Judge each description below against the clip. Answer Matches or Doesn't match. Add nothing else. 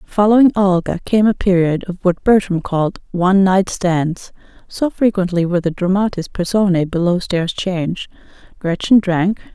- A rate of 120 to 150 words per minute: Matches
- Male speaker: Doesn't match